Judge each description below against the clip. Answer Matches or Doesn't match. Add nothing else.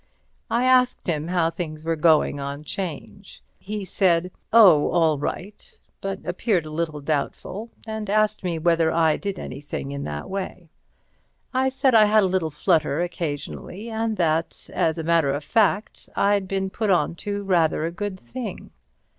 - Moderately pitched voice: Matches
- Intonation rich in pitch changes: Doesn't match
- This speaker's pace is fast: Doesn't match